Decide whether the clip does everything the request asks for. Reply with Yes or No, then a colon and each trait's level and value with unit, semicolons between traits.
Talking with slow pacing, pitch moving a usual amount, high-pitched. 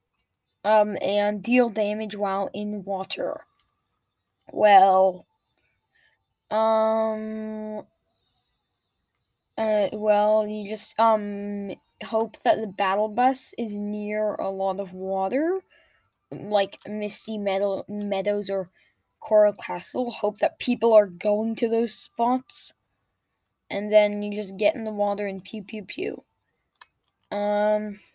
No: slow, 115 wpm; narrow, 1.5 semitones; high, 210 Hz